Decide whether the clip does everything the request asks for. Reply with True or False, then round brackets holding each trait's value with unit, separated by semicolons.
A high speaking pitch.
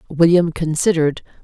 False (165 Hz)